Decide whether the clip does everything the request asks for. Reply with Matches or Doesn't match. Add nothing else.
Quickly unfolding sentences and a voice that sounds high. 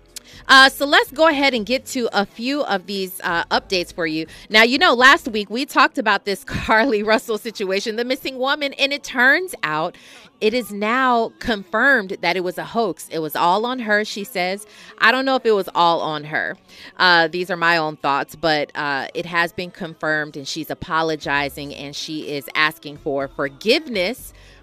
Doesn't match